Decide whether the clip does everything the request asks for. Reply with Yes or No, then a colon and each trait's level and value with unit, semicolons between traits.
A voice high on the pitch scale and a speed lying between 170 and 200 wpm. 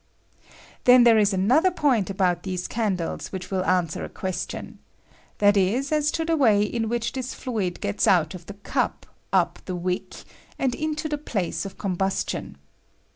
Yes: high, 205 Hz; average, 180 wpm